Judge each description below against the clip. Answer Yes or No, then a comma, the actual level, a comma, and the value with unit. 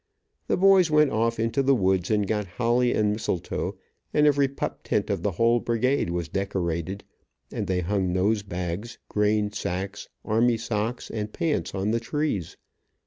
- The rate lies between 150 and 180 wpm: Yes, average, 165 wpm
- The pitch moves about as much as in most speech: Yes, average, 3.9 semitones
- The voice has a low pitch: Yes, low, 105 Hz